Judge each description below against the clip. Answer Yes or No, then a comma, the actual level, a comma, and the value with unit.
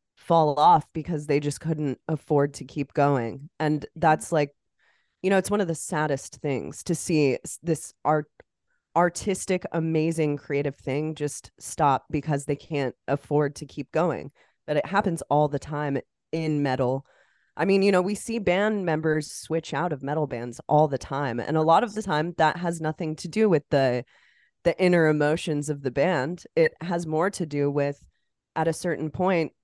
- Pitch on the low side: No, medium, 155 Hz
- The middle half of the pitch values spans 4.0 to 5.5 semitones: No, average, 2.8 semitones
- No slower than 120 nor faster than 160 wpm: No, average, 185 wpm